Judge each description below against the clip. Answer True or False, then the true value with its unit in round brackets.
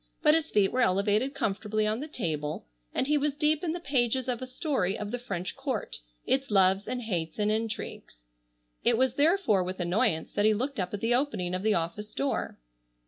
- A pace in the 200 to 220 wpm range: True (205 wpm)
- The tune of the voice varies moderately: False (5.8 semitones)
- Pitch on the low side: False (220 Hz)